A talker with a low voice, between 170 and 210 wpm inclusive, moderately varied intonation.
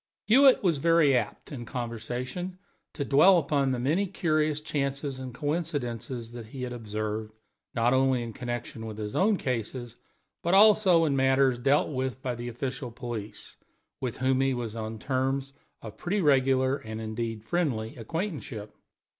No: low, 130 Hz; average, 155 wpm; average, 4.1 semitones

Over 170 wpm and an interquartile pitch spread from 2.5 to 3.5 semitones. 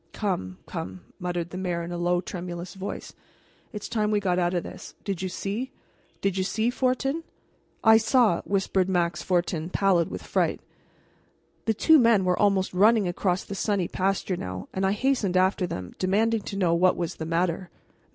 Yes: average, 180 wpm; average, 2.9 semitones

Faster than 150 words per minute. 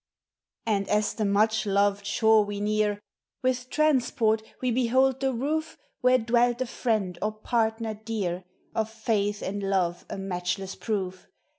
No: average, 145 wpm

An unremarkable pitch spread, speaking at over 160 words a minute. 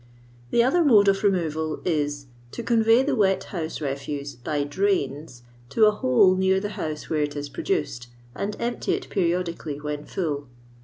No: wide, 6.2 semitones; average, 170 wpm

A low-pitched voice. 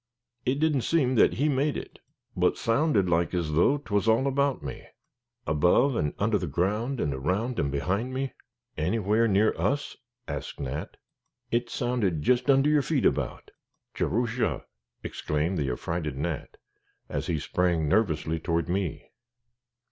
Yes: low, 100 Hz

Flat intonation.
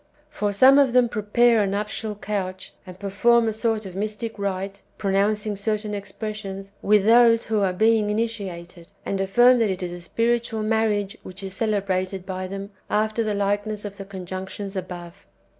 Yes: narrow, 2.3 semitones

